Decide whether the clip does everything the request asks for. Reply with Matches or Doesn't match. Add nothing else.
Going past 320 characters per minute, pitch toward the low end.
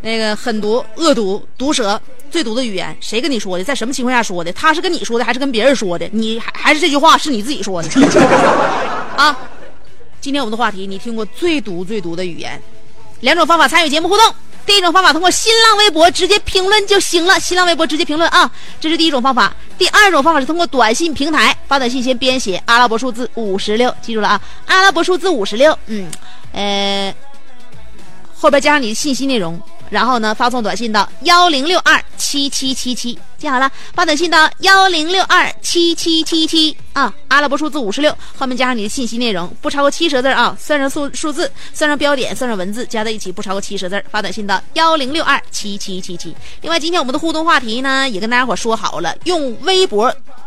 Doesn't match